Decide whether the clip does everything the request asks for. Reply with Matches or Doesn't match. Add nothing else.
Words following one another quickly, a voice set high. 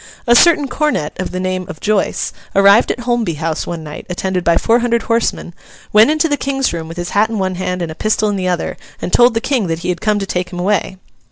Matches